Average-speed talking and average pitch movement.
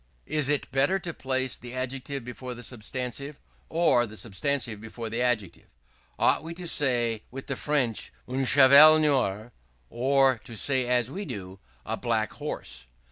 Yes: average, 160 wpm; average, 3.0 semitones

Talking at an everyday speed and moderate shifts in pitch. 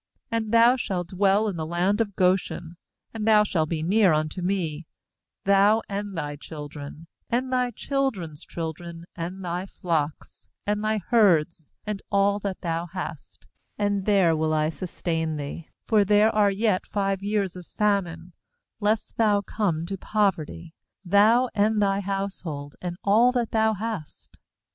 Yes: average, 155 wpm; average, 4.0 semitones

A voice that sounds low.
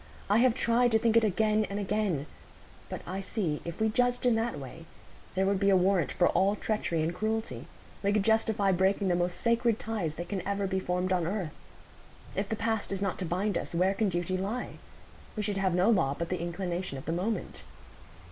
No: high, 195 Hz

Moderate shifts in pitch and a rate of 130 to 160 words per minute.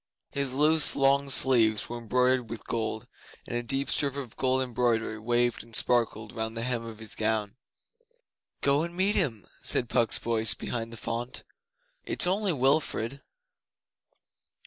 Yes: average, 3.4 semitones; average, 150 wpm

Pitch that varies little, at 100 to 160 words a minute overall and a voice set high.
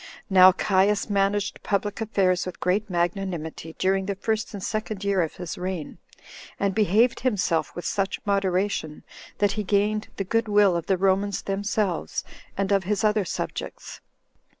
Yes: narrow, 2.1 semitones; average, 155 wpm; high, 195 Hz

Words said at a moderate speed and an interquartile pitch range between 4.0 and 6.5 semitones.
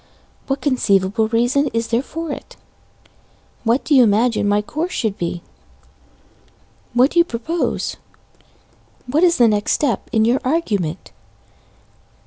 No: slow, 130 wpm; average, 5.0 semitones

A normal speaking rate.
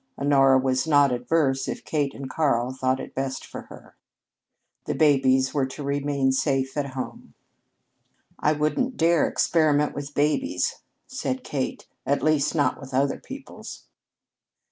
Yes: average, 145 wpm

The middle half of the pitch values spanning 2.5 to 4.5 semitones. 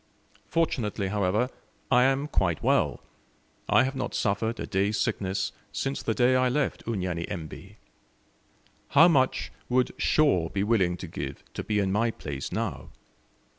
No: average, 5.3 semitones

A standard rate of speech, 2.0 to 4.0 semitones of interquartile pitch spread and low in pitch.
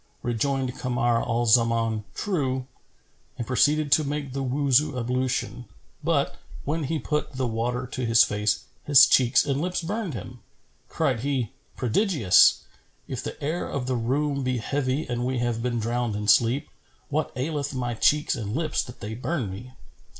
Yes: average, 165 wpm; average, 3.4 semitones; low, 130 Hz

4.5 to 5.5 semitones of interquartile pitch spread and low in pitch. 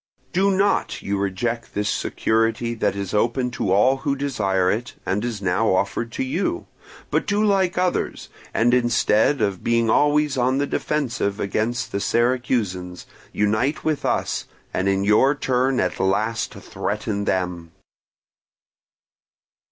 Yes: average, 4.9 semitones; low, 115 Hz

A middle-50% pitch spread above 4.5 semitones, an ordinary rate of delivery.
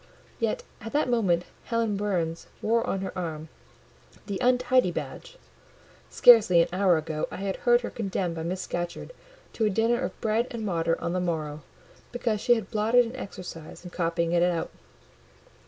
Yes: average, 5.2 semitones; average, 170 wpm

